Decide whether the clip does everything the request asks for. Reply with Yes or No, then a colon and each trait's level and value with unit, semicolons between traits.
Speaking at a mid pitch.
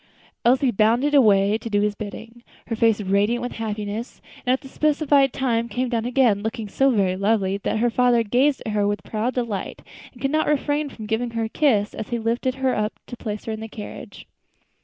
No: high, 230 Hz